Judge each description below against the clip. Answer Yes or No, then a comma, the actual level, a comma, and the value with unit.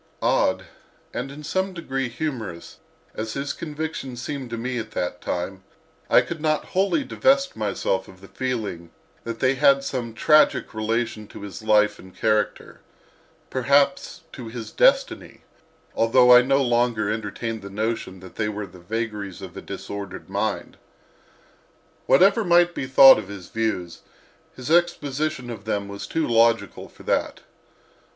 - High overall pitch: No, low, 115 Hz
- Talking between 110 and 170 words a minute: Yes, average, 145 wpm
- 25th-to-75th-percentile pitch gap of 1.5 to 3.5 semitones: No, average, 5.0 semitones